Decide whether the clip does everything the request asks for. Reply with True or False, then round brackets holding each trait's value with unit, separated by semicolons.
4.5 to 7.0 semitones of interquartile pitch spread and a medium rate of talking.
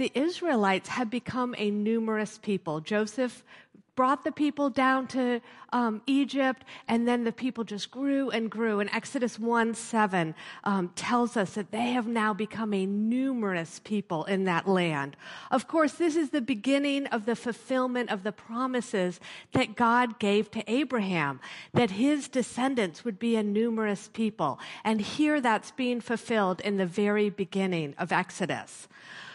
False (3.7 semitones; 160 wpm)